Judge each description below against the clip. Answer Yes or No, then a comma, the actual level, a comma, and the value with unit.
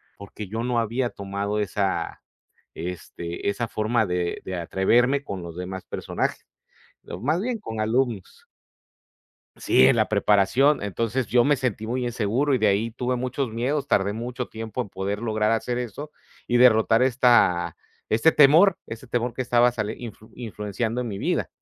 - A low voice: Yes, low, 115 Hz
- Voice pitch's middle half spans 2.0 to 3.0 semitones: No, average, 3.6 semitones